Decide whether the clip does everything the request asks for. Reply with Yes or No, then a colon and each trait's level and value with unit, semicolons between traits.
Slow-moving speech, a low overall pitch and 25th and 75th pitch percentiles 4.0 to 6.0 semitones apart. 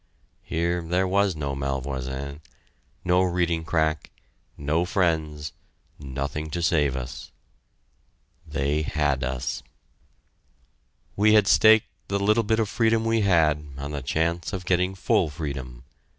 Yes: slow, 125 wpm; very low, 80 Hz; average, 4.8 semitones